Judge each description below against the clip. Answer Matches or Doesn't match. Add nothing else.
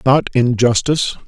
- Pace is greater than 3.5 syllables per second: Matches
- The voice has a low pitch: Matches